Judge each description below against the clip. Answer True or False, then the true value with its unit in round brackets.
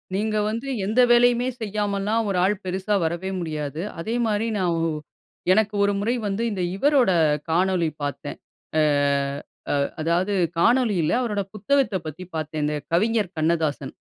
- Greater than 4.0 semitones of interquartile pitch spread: True (4.6 semitones)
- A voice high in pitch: True (195 Hz)